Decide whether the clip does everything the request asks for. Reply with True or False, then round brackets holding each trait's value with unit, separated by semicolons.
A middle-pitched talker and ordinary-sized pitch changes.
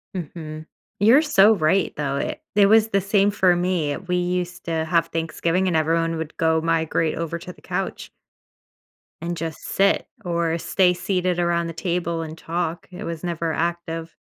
False (170 Hz; 1.9 semitones)